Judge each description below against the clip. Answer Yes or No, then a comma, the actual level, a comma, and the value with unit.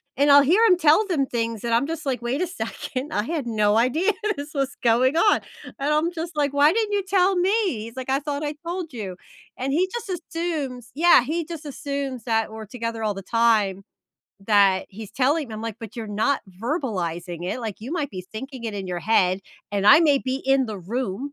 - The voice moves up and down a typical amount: No, wide, 5.9 semitones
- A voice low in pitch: No, very high, 265 Hz